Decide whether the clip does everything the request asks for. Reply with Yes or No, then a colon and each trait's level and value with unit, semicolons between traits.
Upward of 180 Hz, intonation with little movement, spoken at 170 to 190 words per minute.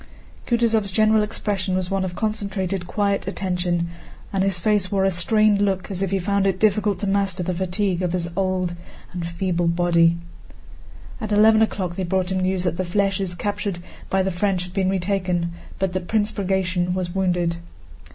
Yes: high, 190 Hz; narrow, 2.1 semitones; average, 180 wpm